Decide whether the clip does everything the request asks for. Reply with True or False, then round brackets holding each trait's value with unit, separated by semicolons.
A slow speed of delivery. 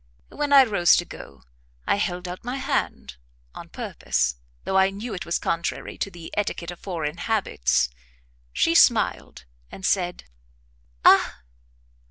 False (145 wpm)